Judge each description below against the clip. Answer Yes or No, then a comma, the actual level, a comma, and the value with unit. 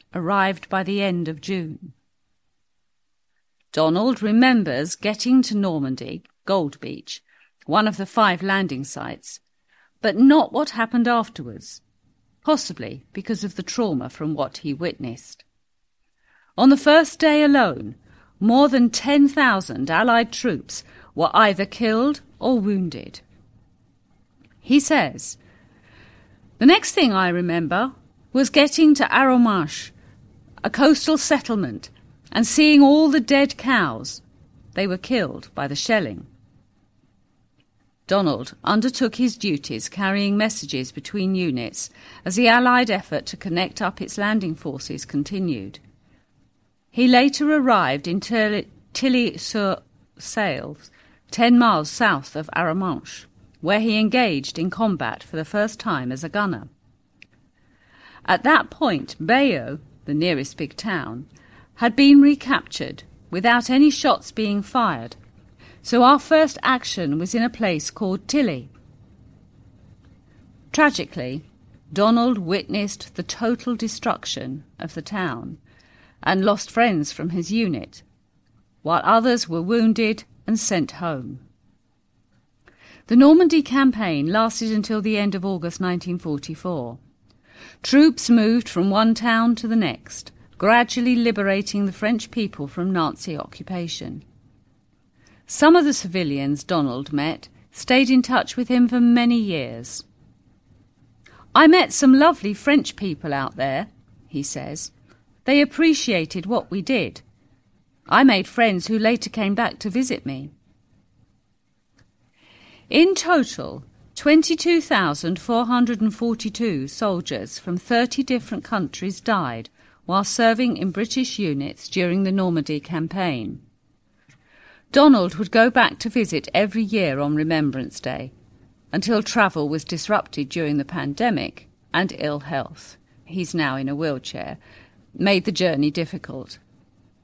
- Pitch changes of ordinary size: No, wide, 8.8 semitones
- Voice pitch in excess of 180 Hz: Yes, high, 190 Hz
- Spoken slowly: Yes, slow, 120 wpm